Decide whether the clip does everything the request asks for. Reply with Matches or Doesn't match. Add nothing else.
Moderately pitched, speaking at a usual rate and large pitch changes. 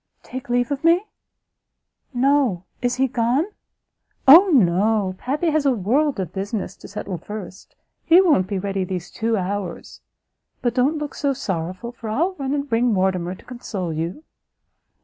Doesn't match